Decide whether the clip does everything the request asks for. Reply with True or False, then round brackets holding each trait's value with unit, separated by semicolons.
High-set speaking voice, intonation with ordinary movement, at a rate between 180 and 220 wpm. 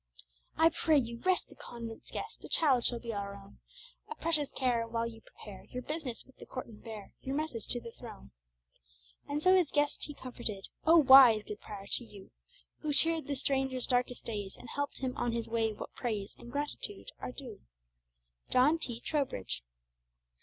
True (250 Hz; 4.3 semitones; 190 wpm)